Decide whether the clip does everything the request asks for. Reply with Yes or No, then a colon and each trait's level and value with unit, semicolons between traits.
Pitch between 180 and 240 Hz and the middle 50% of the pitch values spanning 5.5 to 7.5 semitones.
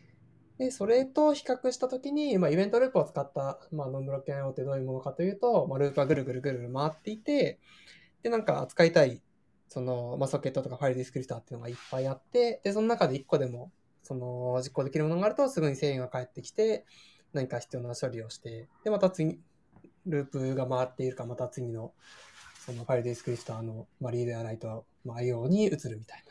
No: low, 135 Hz; wide, 6.4 semitones